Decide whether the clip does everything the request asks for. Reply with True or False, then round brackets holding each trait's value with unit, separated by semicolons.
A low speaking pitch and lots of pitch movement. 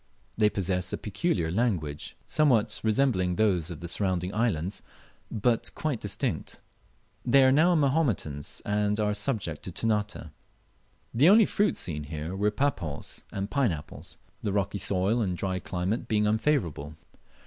False (105 Hz; 4.8 semitones)